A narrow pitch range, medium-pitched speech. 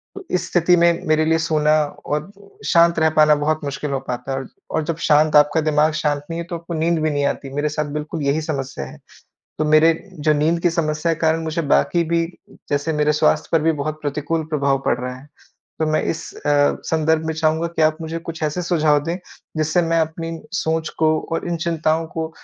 Yes: narrow, 1.7 semitones; medium, 155 Hz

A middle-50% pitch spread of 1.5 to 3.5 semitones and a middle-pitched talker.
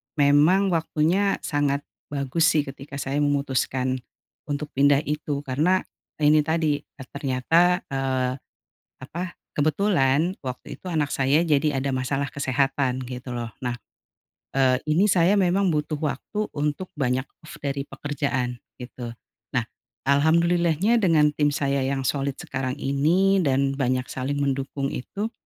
Yes: average, 3.1 semitones; medium, 145 Hz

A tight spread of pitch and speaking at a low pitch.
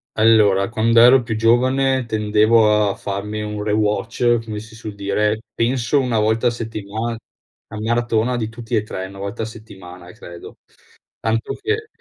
Yes: narrow, 1.9 semitones; low, 110 Hz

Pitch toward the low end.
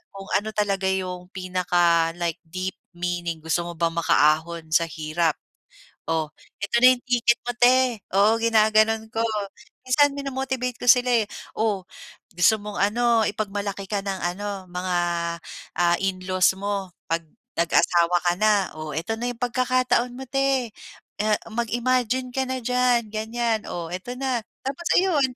No: high, 205 Hz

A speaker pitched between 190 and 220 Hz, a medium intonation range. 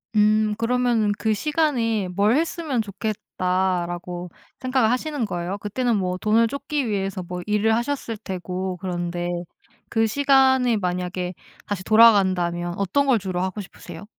Yes: high, 210 Hz; average, 4.7 semitones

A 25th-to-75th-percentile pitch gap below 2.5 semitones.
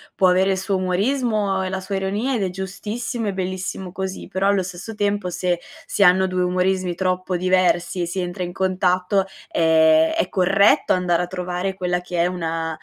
Yes: narrow, 1.3 semitones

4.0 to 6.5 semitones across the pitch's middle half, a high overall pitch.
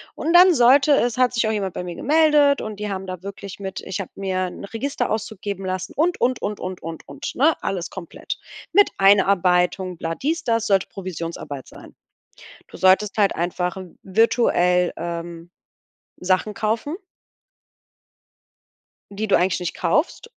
Yes: average, 4.3 semitones; high, 195 Hz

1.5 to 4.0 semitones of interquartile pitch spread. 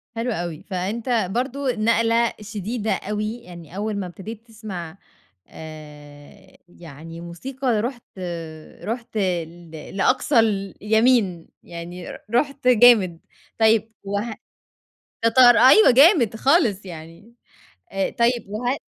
No: average, 5.2 semitones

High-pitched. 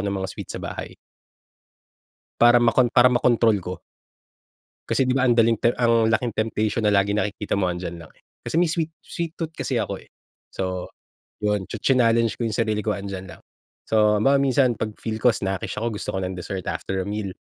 No: low, 110 Hz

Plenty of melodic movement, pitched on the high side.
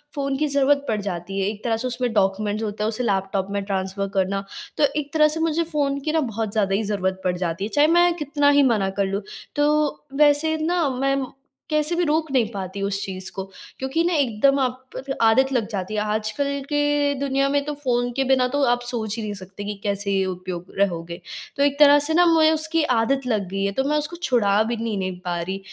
Yes: wide, 6.4 semitones; high, 230 Hz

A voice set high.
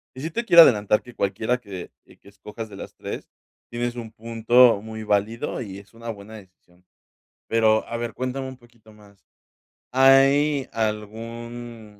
No: low, 115 Hz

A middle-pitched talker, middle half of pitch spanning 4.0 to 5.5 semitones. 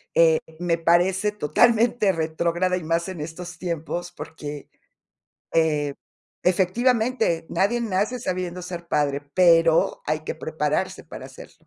No: medium, 175 Hz; average, 2.9 semitones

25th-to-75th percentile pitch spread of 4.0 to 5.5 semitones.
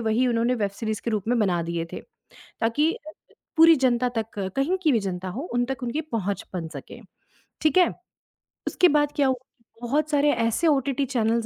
Yes: average, 4.7 semitones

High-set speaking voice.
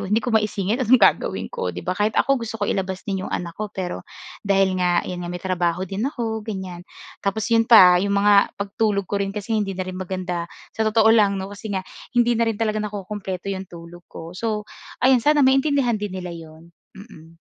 Yes: high, 200 Hz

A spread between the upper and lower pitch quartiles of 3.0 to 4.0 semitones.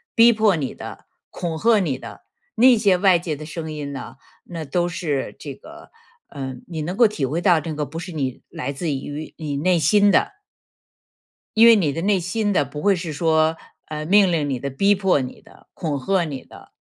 No: average, 4.8 semitones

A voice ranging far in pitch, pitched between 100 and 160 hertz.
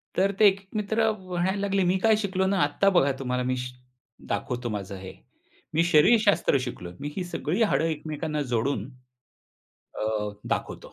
No: wide, 7.4 semitones; medium, 175 Hz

